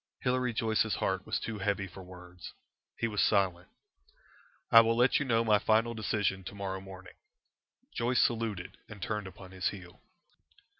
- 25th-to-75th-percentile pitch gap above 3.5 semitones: No, average, 3.2 semitones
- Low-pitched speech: Yes, low, 105 Hz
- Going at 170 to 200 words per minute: No, average, 160 wpm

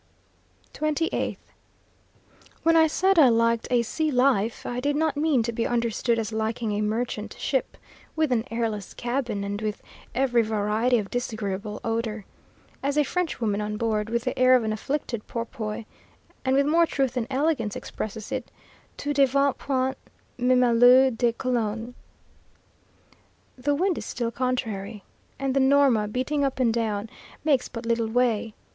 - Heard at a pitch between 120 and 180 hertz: No, high, 240 Hz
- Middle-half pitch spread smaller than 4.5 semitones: Yes, average, 3.6 semitones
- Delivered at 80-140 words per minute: No, average, 160 wpm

